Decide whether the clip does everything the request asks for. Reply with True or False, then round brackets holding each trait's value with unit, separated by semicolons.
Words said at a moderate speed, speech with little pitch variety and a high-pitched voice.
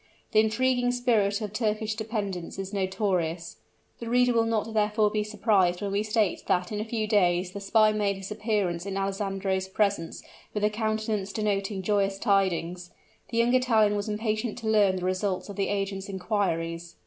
True (175 wpm; 2.1 semitones; 205 Hz)